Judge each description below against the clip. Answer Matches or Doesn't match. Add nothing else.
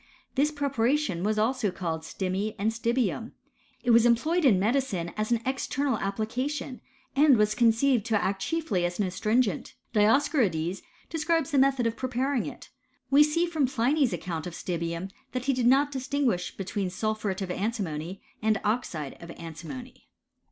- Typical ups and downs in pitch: Doesn't match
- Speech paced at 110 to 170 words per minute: Matches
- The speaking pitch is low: Doesn't match